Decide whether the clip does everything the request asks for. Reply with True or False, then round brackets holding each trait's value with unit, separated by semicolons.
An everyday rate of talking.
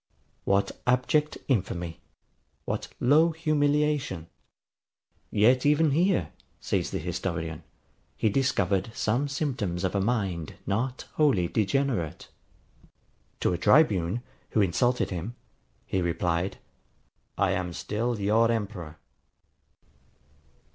False (100 wpm)